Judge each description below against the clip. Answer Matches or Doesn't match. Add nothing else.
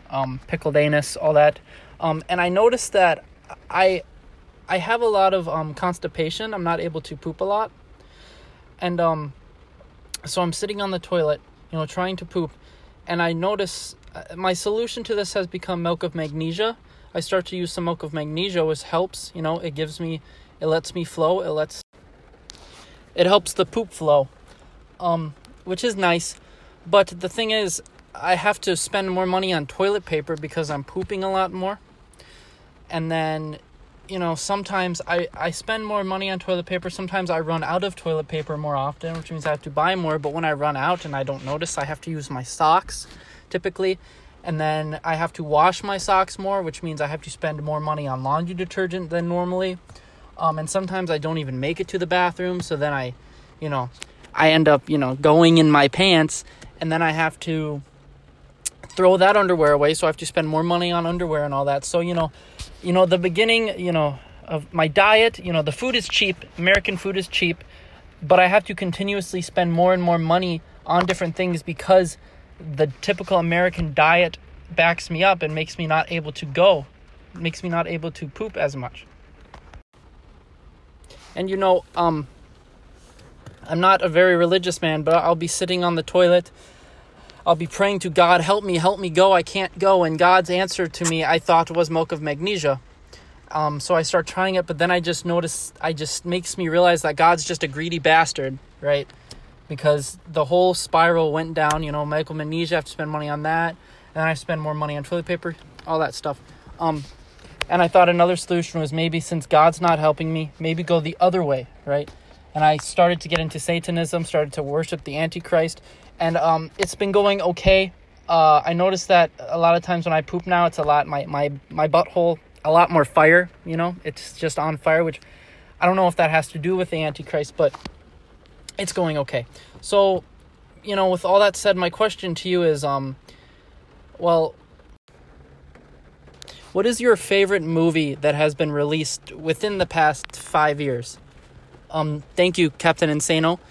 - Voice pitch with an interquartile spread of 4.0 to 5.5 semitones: Doesn't match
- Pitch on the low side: Doesn't match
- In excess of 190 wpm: Matches